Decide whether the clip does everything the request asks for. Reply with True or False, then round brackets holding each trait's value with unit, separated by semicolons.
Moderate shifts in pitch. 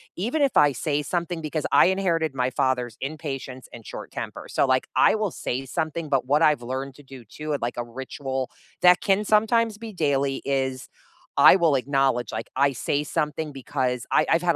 True (4.1 semitones)